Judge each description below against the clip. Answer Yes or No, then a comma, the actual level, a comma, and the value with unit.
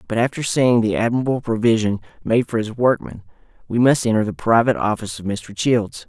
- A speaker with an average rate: Yes, average, 190 wpm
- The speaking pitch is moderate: No, low, 115 Hz